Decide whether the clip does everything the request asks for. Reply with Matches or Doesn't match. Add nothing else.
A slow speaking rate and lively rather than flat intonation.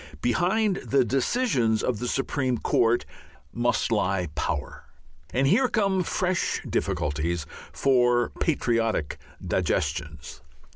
Matches